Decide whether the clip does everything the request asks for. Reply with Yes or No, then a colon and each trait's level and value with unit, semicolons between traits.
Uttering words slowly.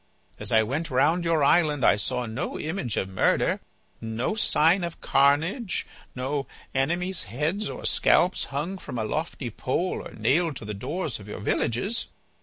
No: average, 165 wpm